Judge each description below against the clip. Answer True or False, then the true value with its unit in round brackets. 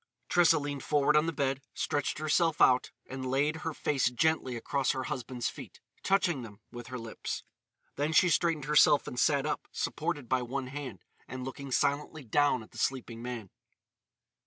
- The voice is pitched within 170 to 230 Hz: False (140 Hz)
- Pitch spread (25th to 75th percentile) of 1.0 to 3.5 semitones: True (3.1 semitones)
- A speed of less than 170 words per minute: False (175 wpm)